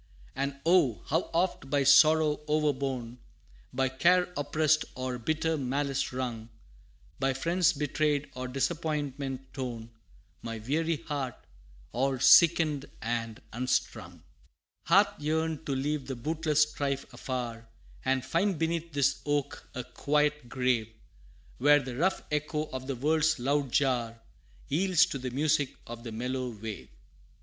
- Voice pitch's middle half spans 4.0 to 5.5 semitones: No, average, 3.2 semitones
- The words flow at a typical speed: No, slow, 130 wpm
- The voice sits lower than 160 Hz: Yes, medium, 140 Hz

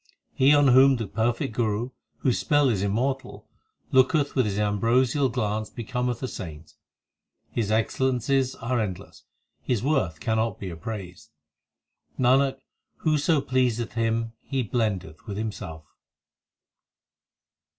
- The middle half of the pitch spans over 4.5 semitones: No, average, 3.8 semitones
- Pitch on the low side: Yes, low, 120 Hz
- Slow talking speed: Yes, slow, 120 wpm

